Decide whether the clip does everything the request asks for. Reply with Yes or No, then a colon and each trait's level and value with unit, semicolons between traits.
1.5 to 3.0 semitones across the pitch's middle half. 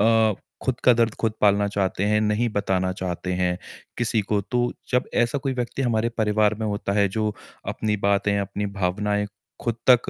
Yes: narrow, 2.4 semitones